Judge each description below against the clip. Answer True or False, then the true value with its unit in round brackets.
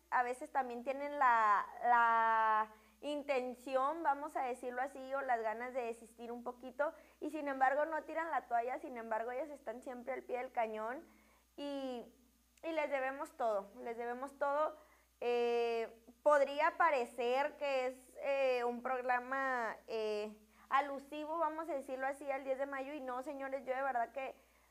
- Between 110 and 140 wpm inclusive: False (165 wpm)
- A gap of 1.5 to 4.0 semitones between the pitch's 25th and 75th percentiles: True (3.0 semitones)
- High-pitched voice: True (260 Hz)